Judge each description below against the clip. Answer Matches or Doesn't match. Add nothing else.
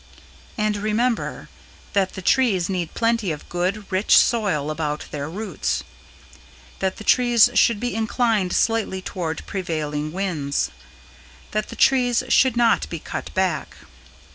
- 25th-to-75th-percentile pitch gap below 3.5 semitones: Doesn't match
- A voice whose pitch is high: Matches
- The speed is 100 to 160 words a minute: Matches